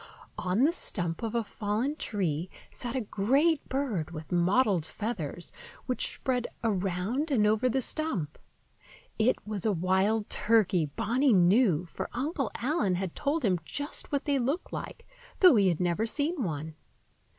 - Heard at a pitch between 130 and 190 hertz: No, high, 215 Hz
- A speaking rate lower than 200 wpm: Yes, average, 155 wpm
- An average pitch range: No, wide, 6.4 semitones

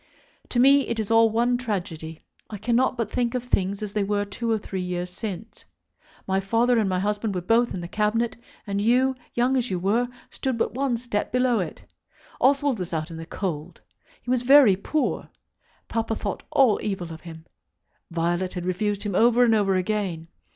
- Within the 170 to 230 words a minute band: Yes, average, 195 wpm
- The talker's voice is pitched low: No, high, 210 Hz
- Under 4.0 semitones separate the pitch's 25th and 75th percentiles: No, average, 4.6 semitones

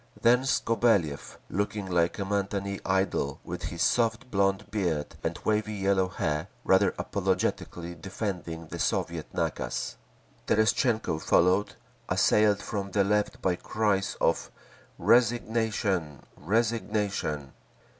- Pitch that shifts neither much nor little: Yes, average, 3.3 semitones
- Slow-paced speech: Yes, slow, 110 wpm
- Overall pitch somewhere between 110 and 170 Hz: No, low, 100 Hz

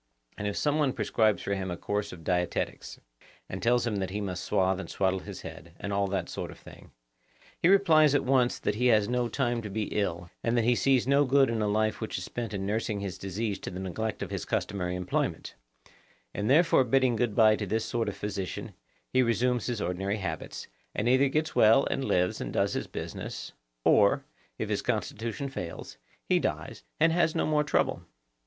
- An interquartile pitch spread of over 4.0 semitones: Yes, average, 4.4 semitones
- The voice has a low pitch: Yes, low, 110 Hz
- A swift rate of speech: Yes, fast, 210 wpm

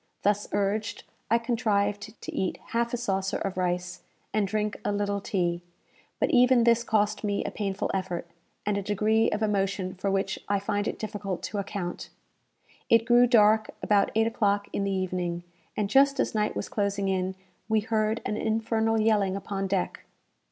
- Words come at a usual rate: Yes, average, 175 wpm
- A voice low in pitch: No, high, 205 Hz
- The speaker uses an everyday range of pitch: No, narrow, 2.2 semitones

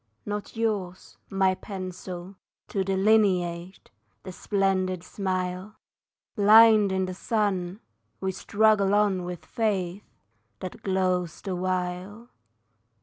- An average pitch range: No, narrow, 2.0 semitones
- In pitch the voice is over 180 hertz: Yes, high, 190 Hz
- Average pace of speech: No, slow, 100 wpm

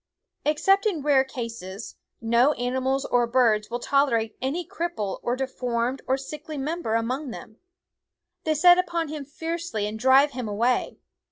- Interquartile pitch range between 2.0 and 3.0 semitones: No, average, 4.6 semitones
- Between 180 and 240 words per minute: No, average, 150 wpm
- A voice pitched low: No, very high, 265 Hz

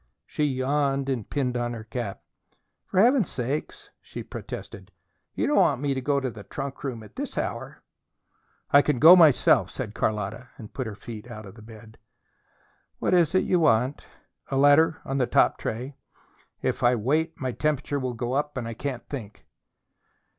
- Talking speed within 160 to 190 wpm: Yes, average, 180 wpm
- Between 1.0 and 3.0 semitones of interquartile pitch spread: No, average, 3.9 semitones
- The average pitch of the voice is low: Yes, low, 130 Hz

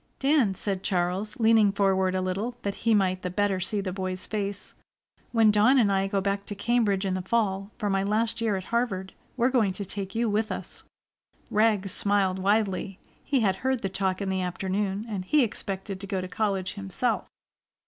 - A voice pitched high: Yes, high, 200 Hz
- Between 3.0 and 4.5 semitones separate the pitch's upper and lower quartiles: No, narrow, 2.4 semitones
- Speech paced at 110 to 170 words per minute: No, average, 200 wpm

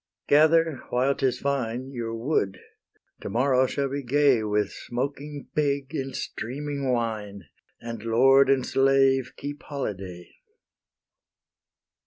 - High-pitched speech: No, low, 135 Hz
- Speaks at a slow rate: Yes, slow, 115 wpm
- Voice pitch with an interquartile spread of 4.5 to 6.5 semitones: No, average, 3.3 semitones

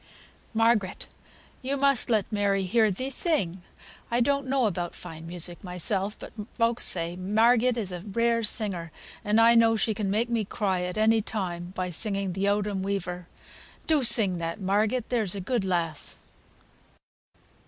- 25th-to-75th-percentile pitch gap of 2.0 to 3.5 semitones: No, average, 4.1 semitones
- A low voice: No, high, 205 Hz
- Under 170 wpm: Yes, average, 160 wpm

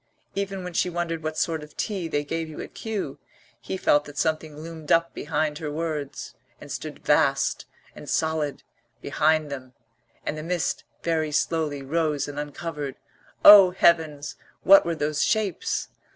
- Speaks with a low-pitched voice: No, medium, 155 Hz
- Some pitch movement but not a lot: No, narrow, 2.2 semitones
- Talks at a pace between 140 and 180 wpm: Yes, average, 160 wpm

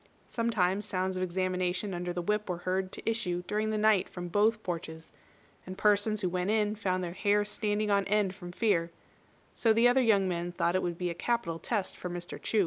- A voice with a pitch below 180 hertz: No, high, 190 Hz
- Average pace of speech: No, fast, 215 wpm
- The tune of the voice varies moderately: Yes, average, 3.0 semitones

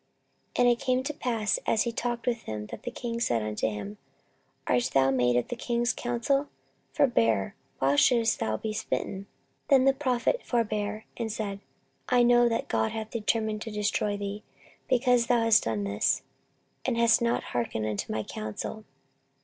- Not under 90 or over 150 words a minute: No, average, 175 wpm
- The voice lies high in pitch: Yes, high, 220 Hz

